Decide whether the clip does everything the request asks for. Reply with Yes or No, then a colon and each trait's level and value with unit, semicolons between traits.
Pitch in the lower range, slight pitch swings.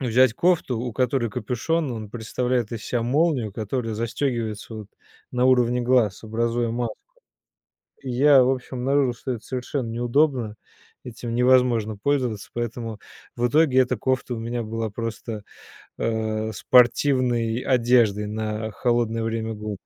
Yes: low, 120 Hz; narrow, 2.3 semitones